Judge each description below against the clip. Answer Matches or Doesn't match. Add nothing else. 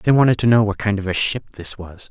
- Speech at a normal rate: Doesn't match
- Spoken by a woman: Doesn't match